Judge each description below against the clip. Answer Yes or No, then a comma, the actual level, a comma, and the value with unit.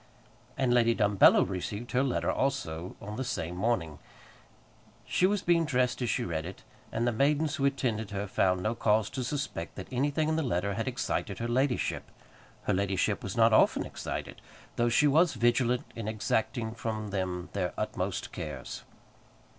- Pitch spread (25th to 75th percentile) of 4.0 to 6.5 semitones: Yes, average, 5.0 semitones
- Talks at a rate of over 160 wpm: Yes, average, 170 wpm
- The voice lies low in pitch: Yes, low, 115 Hz